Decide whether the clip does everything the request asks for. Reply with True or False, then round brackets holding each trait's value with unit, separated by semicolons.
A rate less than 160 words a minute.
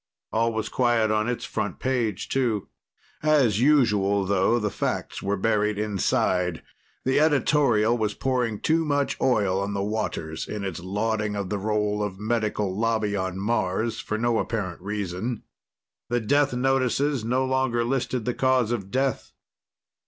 True (150 wpm)